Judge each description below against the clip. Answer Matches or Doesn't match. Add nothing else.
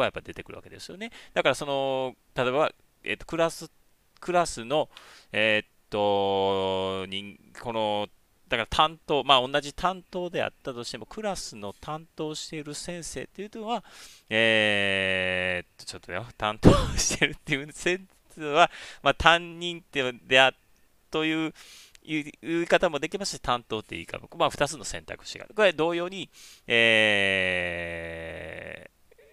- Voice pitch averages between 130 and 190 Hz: Matches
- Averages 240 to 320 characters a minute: Matches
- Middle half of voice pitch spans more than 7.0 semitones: Matches